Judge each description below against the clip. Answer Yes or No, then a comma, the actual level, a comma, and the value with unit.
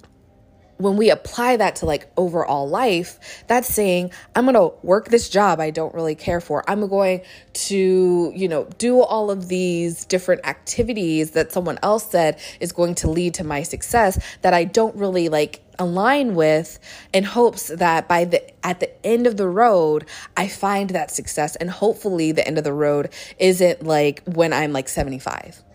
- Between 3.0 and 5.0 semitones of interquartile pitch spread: Yes, average, 4.2 semitones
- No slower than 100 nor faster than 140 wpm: No, average, 180 wpm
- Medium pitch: Yes, medium, 180 Hz